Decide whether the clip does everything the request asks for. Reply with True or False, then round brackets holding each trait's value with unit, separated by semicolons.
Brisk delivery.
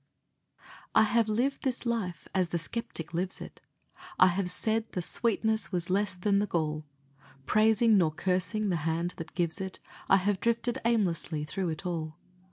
False (170 wpm)